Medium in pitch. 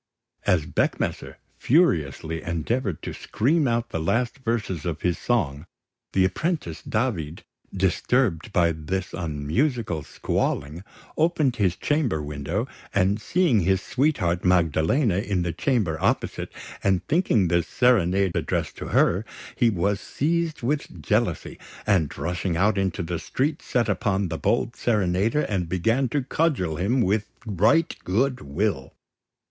No: low, 100 Hz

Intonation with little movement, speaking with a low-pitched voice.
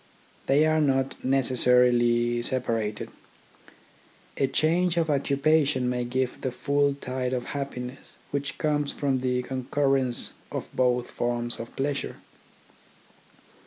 Yes: narrow, 2.3 semitones; low, 130 Hz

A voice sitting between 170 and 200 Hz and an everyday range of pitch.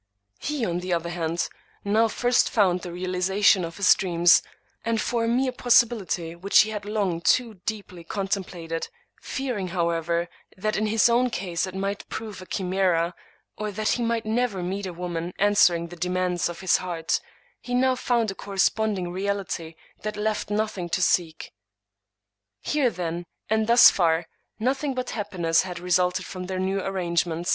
Yes: high, 190 Hz; average, 3.7 semitones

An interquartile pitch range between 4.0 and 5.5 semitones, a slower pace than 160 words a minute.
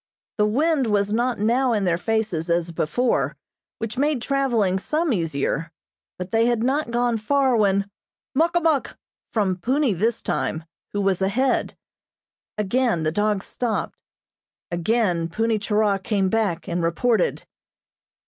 Yes: average, 4.7 semitones; average, 140 wpm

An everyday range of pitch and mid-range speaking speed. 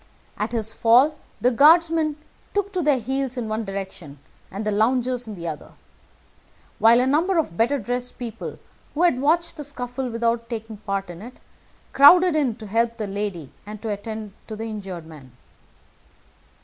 Yes: average, 4.5 semitones; average, 175 wpm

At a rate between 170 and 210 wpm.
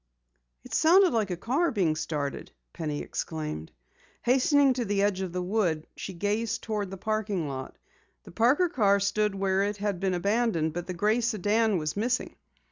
Yes: average, 175 wpm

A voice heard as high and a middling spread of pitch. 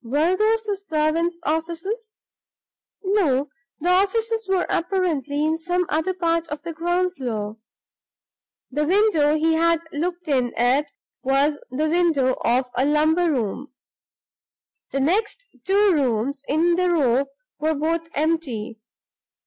Yes: very high, 320 Hz; average, 4.2 semitones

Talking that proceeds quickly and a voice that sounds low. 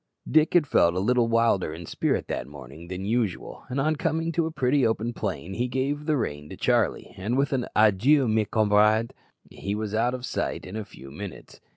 Yes: fast, 210 wpm; low, 115 Hz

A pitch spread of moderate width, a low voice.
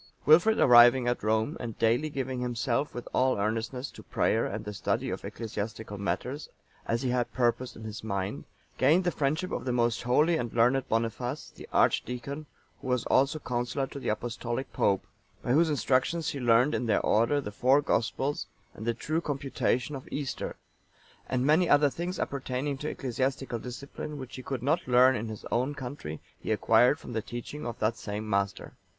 Yes: average, 3.5 semitones; low, 125 Hz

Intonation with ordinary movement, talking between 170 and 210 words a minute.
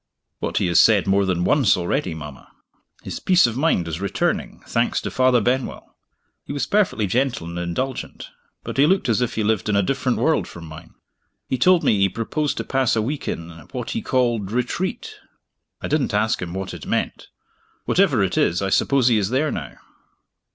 No: wide, 6.2 semitones; average, 200 wpm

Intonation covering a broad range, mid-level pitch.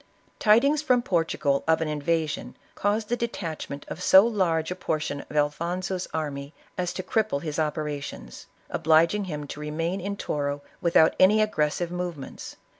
No: average, 4.3 semitones; medium, 165 Hz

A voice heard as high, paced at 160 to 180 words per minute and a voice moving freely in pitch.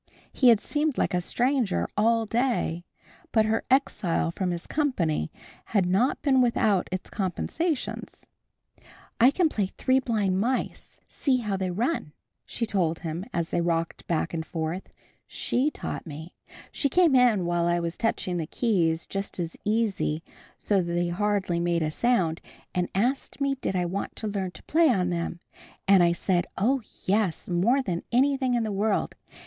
Yes: high, 195 Hz; average, 170 wpm; wide, 6.0 semitones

